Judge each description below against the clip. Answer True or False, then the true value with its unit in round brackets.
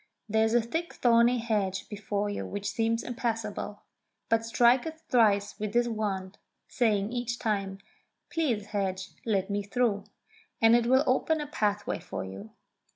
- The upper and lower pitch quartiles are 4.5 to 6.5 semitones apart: False (2.9 semitones)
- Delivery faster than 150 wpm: True (160 wpm)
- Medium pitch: False (220 Hz)